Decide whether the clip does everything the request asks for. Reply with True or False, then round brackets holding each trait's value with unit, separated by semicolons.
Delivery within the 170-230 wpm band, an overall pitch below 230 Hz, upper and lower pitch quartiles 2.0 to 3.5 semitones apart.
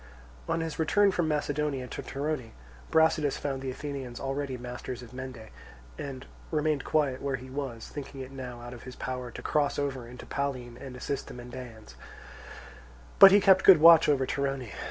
True (175 wpm; 135 Hz; 3.0 semitones)